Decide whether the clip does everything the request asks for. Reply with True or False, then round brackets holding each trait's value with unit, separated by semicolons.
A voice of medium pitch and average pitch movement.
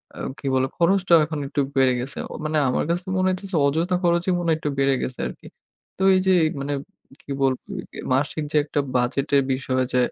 True (150 Hz; 4.2 semitones)